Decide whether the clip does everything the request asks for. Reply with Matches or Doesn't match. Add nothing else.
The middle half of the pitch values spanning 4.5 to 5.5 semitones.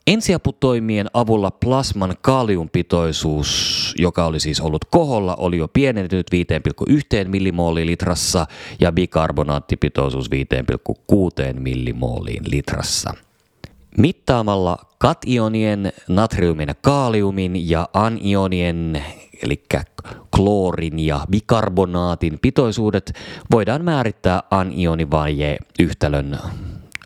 Matches